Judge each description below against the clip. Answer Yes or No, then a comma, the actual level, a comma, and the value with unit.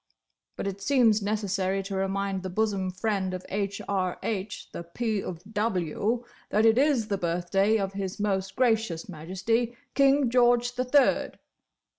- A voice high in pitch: Yes, high, 200 Hz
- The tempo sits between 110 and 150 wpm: Yes, average, 145 wpm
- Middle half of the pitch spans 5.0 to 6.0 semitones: No, average, 3.2 semitones